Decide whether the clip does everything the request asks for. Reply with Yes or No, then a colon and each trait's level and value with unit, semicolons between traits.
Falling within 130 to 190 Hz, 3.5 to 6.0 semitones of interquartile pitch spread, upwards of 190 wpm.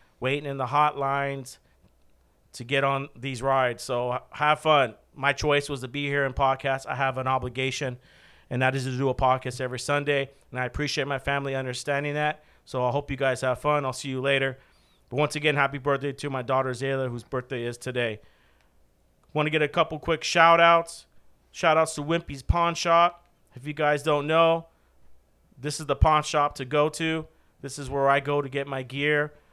No: medium, 140 Hz; narrow, 2.4 semitones; fast, 205 wpm